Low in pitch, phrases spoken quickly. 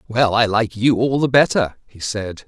Yes: low, 115 Hz; fast, 220 wpm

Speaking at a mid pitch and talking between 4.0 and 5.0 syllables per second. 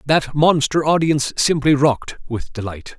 Yes: medium, 145 Hz; 4.9 syllables/s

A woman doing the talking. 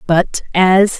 Yes: female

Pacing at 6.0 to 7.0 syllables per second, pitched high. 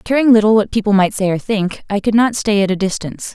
Yes: 6.1 syllables/s; high, 205 Hz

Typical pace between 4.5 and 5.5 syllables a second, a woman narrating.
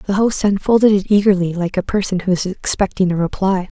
No: 5.7 syllables/s; female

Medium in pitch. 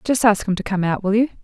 No: high, 210 Hz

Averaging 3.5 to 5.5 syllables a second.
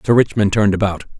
No: 7.2 syllables/s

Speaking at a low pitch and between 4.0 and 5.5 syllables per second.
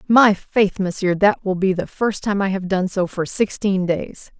No: high, 195 Hz; 4.3 syllables/s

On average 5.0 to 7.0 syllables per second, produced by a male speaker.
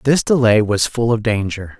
No: 4.6 syllables/s; male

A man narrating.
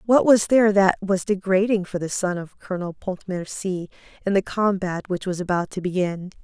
No: female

